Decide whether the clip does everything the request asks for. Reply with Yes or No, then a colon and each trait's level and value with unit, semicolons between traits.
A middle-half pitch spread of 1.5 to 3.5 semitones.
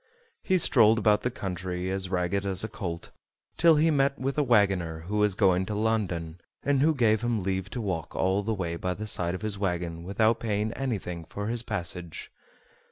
No: average, 3.9 semitones